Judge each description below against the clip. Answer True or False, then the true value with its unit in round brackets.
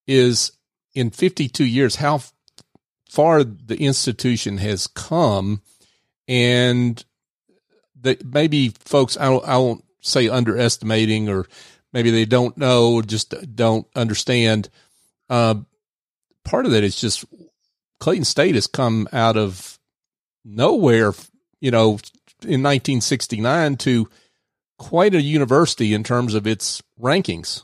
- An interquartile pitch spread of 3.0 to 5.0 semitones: True (3.5 semitones)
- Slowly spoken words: True (115 wpm)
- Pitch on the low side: True (120 Hz)